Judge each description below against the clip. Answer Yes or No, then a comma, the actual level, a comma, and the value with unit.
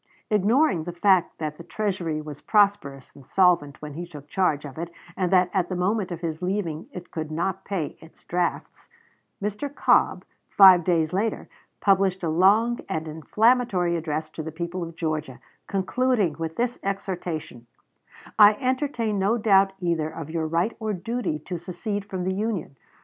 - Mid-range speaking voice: Yes, medium, 180 Hz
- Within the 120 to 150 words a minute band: No, average, 170 wpm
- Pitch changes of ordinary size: Yes, average, 4.1 semitones